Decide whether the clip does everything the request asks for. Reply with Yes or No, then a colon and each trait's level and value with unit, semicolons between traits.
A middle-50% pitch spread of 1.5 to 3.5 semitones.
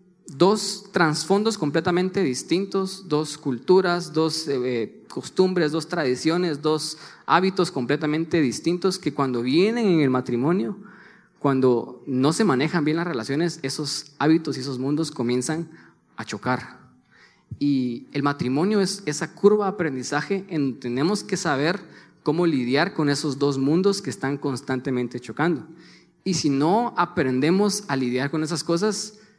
No: average, 4.6 semitones